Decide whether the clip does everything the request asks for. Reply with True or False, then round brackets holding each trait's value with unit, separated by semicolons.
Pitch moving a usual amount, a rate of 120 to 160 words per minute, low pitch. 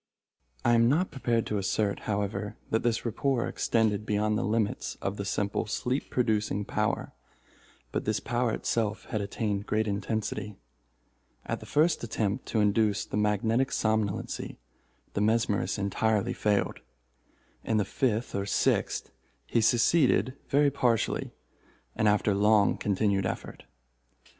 False (2.2 semitones; 135 wpm; 110 Hz)